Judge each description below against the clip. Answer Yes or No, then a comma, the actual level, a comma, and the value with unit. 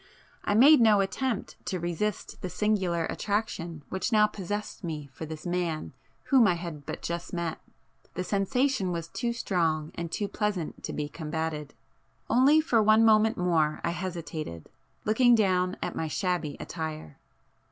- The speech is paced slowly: No, average, 150 wpm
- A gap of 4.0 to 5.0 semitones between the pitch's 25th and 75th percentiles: Yes, average, 4.7 semitones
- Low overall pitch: No, medium, 180 Hz